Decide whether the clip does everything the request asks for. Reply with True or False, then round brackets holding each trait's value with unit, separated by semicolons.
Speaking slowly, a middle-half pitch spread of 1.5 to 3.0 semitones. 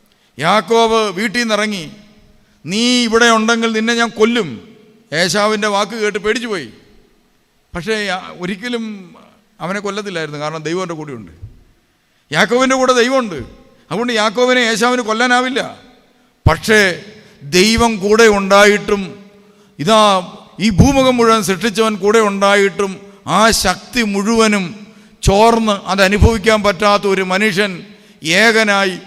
True (100 wpm; 2.5 semitones)